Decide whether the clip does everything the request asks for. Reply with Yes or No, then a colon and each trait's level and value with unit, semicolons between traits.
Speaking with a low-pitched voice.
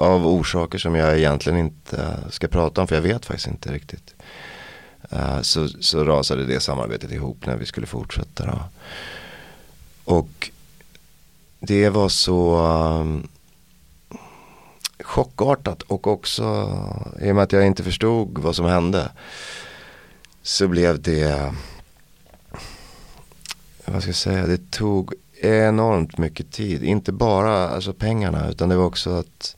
Yes: very low, 90 Hz